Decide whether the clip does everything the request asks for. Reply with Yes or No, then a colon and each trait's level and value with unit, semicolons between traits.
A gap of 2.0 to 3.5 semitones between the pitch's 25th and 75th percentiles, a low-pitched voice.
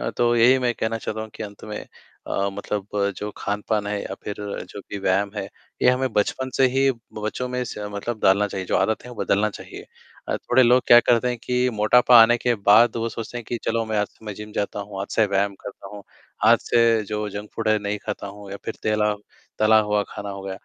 Yes: average, 2.7 semitones; low, 105 Hz